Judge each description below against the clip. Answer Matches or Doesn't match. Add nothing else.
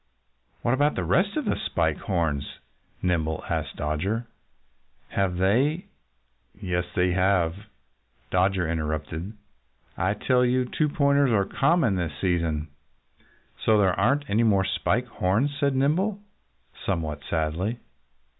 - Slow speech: Matches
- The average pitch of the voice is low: Matches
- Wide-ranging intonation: Matches